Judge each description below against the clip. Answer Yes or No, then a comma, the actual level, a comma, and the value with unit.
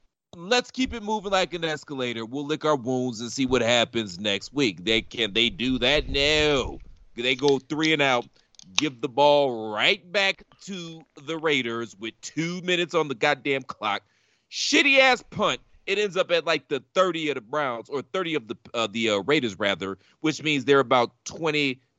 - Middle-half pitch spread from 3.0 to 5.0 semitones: No, wide, 5.4 semitones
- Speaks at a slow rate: No, average, 195 wpm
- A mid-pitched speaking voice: Yes, medium, 145 Hz